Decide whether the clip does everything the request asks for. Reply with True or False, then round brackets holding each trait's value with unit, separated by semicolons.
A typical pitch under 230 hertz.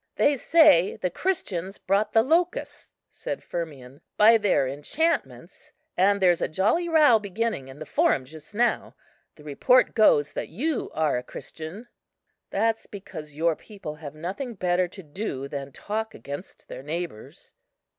True (185 Hz)